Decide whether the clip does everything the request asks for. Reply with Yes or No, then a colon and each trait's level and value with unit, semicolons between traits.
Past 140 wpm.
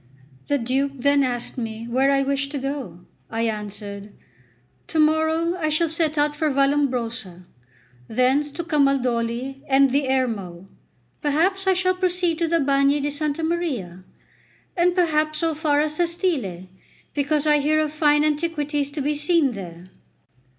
Yes: average, 150 wpm